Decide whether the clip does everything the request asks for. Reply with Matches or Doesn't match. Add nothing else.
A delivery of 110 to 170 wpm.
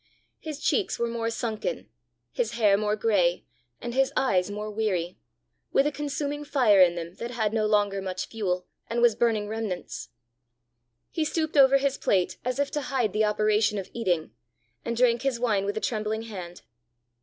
Doesn't match